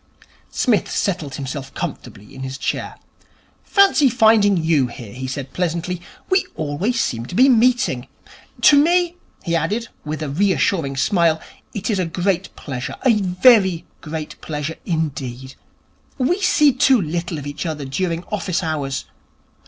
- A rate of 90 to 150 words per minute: Yes, average, 145 wpm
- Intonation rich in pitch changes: Yes, wide, 6.8 semitones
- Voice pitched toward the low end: No, medium, 170 Hz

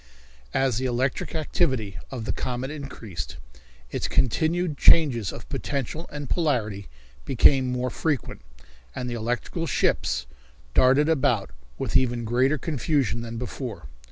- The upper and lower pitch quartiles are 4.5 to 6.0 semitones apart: No, average, 3.9 semitones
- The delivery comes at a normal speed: No, slow, 130 wpm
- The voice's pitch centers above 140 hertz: No, low, 130 Hz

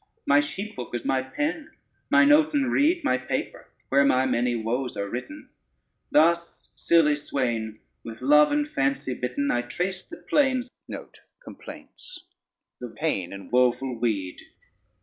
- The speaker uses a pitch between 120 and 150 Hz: Yes, low, 135 Hz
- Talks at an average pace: No, slow, 130 wpm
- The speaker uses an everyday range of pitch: No, wide, 7.6 semitones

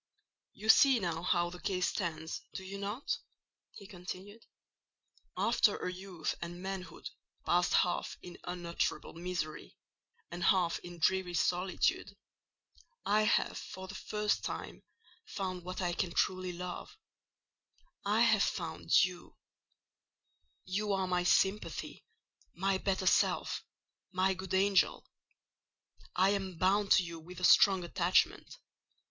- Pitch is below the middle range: No, medium, 185 Hz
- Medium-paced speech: No, slow, 120 wpm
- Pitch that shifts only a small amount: Yes, narrow, 1.7 semitones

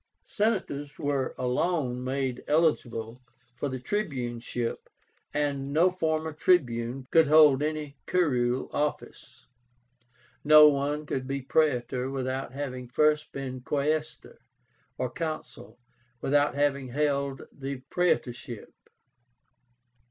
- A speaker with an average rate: No, slow, 100 wpm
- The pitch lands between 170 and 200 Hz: No, medium, 140 Hz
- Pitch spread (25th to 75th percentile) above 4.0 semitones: No, average, 3.1 semitones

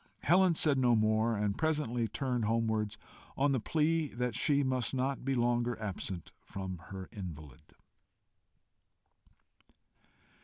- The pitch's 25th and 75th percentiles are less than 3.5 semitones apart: No, average, 4.3 semitones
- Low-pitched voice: Yes, low, 120 Hz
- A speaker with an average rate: No, slow, 120 wpm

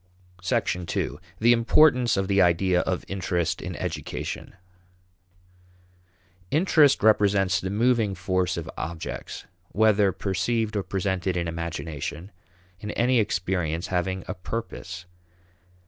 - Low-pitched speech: Yes, very low, 95 Hz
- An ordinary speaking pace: No, slow, 110 wpm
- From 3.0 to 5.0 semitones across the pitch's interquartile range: Yes, average, 3.6 semitones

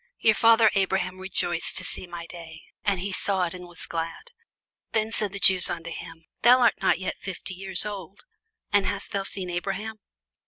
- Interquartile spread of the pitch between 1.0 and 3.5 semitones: Yes, narrow, 2.6 semitones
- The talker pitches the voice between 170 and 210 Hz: Yes, high, 190 Hz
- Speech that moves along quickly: No, average, 190 wpm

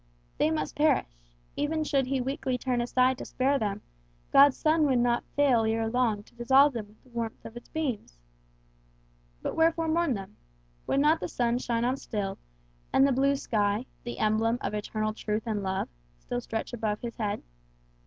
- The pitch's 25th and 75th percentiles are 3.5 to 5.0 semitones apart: Yes, average, 4.2 semitones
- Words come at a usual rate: Yes, average, 185 wpm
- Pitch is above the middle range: Yes, high, 240 Hz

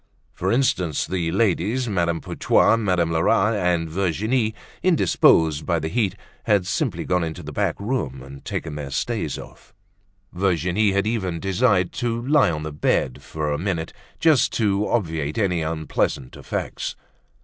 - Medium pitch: No, very low, 90 Hz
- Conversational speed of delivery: Yes, average, 150 wpm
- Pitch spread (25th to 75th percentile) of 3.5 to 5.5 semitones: Yes, average, 5.0 semitones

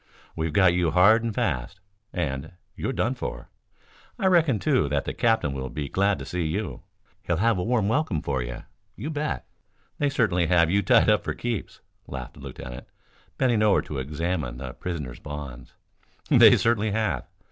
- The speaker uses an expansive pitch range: Yes, wide, 7.5 semitones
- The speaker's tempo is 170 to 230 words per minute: Yes, average, 180 wpm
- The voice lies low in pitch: Yes, very low, 90 Hz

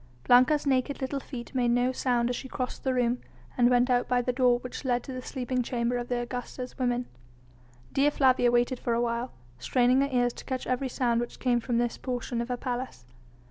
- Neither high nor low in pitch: No, high, 245 Hz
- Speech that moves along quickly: Yes, fast, 220 wpm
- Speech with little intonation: Yes, narrow, 1.1 semitones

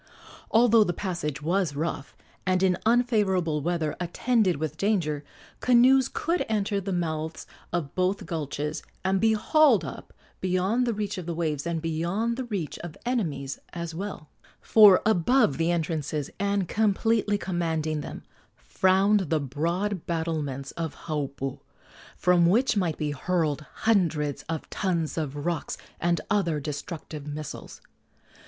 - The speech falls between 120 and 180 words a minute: Yes, average, 140 wpm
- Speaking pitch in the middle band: Yes, medium, 175 Hz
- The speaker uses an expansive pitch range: No, average, 4.8 semitones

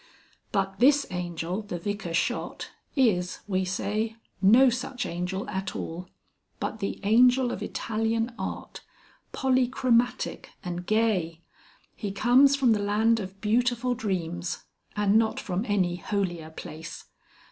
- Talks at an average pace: No, slow, 125 wpm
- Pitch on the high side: Yes, high, 205 Hz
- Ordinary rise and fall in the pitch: Yes, average, 4.8 semitones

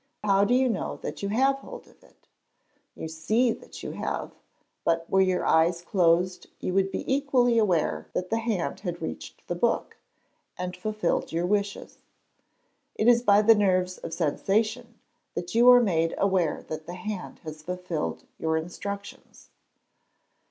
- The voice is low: No, high, 190 Hz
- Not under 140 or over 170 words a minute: Yes, average, 160 wpm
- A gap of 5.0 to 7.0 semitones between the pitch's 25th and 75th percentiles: No, average, 4.5 semitones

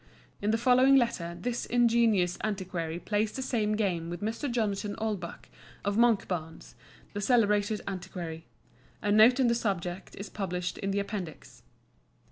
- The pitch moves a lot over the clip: No, average, 4.2 semitones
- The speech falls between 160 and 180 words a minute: No, average, 145 wpm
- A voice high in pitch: Yes, high, 205 Hz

